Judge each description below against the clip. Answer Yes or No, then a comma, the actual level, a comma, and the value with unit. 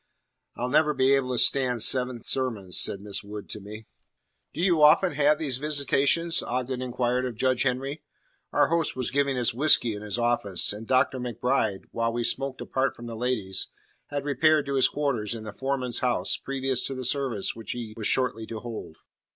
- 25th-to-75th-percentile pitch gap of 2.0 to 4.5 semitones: Yes, average, 3.1 semitones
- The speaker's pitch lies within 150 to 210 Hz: No, low, 125 Hz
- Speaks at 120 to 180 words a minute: No, average, 190 wpm